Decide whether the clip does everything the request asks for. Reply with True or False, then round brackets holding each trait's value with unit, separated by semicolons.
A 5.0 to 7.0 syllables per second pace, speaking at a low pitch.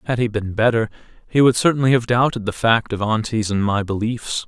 True (5.6 syllables/s; 115 Hz)